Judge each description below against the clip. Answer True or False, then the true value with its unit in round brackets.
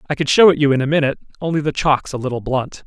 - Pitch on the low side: False (145 Hz)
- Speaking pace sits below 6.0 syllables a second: False (7.4 syllables/s)